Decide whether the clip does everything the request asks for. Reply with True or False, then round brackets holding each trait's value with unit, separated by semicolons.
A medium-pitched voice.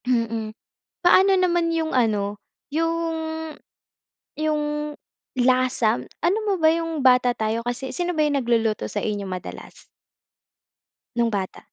False (265 Hz)